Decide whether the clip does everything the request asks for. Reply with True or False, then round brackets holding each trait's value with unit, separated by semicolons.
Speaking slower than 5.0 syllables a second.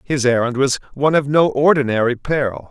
False (5.7 syllables/s)